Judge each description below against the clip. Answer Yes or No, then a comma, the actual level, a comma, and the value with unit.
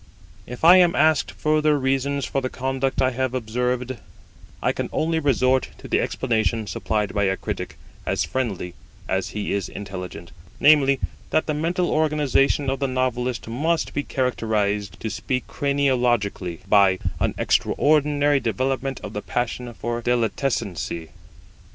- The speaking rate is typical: Yes, average, 145 wpm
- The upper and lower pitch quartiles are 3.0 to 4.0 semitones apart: No, average, 4.4 semitones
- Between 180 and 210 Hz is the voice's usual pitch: No, low, 130 Hz